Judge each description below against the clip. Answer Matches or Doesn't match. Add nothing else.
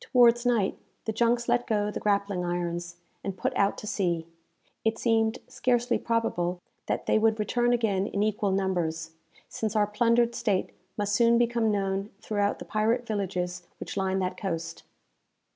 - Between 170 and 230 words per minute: Doesn't match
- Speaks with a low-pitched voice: Doesn't match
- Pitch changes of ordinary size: Matches